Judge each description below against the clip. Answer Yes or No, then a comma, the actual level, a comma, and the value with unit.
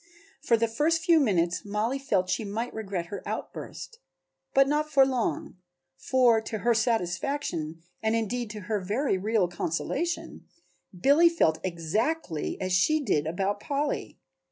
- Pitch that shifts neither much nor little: No, wide, 6.8 semitones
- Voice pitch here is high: Yes, high, 220 Hz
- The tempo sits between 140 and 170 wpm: Yes, average, 145 wpm